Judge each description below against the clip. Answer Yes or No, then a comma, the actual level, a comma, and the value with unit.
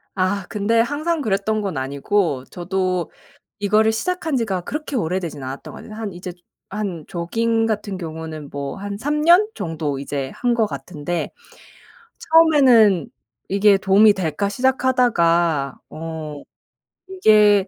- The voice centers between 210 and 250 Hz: No, high, 200 Hz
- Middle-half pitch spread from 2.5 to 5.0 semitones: No, wide, 5.4 semitones